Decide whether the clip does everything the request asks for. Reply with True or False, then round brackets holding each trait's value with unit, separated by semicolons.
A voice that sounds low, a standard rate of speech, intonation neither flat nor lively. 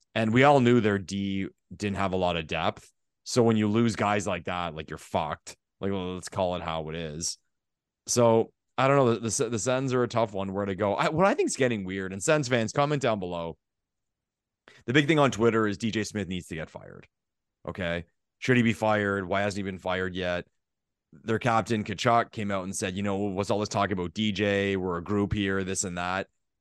False (100 Hz; 230 wpm; 3.6 semitones)